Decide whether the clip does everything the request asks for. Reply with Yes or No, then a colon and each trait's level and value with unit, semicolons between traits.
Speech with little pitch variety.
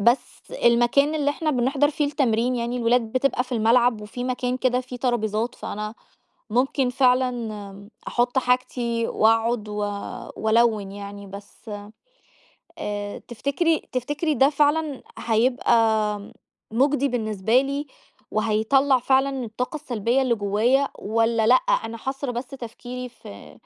No: average, 3.3 semitones